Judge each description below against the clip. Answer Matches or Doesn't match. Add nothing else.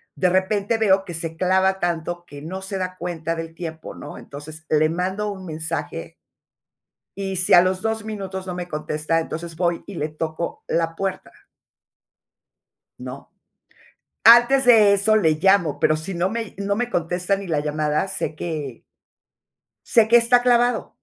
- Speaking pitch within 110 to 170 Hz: Doesn't match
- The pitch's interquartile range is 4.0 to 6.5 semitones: Doesn't match